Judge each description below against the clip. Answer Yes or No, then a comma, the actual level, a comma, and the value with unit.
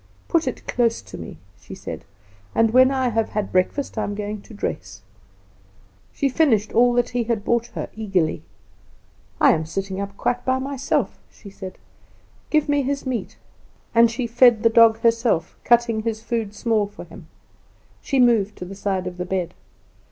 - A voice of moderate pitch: No, high, 225 Hz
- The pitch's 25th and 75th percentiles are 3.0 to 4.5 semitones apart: Yes, average, 3.4 semitones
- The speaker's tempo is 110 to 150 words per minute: No, average, 175 wpm